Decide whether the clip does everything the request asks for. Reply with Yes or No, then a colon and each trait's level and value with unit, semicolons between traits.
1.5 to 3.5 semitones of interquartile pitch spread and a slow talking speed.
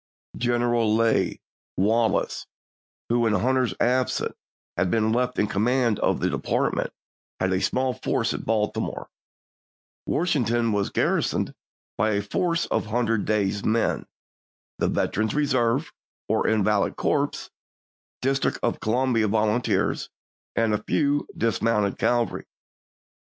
Yes: average, 2.8 semitones; slow, 120 wpm